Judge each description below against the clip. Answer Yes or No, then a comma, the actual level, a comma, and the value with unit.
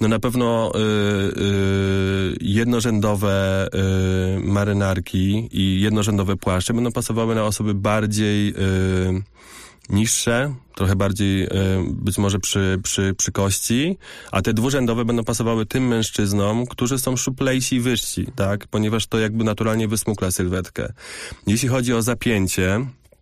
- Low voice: Yes, low, 105 Hz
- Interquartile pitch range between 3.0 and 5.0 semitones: Yes, average, 3.3 semitones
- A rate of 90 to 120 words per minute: No, average, 130 wpm